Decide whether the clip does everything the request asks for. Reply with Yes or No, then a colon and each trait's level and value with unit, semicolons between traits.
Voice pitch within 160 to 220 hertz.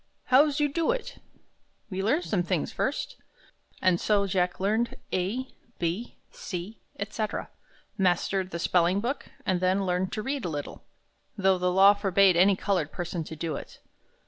Yes: high, 190 Hz